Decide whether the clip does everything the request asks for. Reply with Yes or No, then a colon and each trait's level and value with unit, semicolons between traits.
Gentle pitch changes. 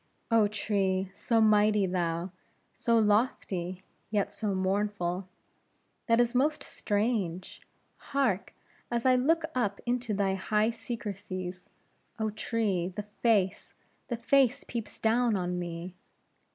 No: average, 3.7 semitones